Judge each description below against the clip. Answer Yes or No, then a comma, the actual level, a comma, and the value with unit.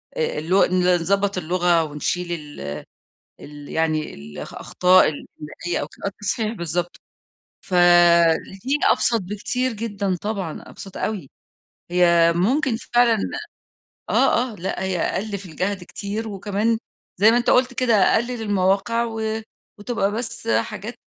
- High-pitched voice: Yes, high, 195 Hz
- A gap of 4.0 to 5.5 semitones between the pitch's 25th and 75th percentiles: Yes, average, 4.3 semitones